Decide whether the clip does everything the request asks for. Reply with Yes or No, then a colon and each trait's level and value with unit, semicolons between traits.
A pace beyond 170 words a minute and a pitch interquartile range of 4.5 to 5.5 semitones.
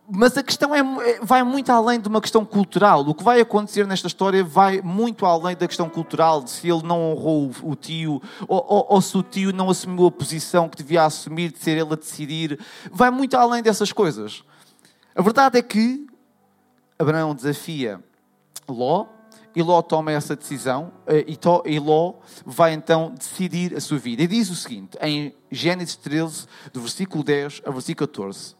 Yes: average, 180 wpm; average, 5.1 semitones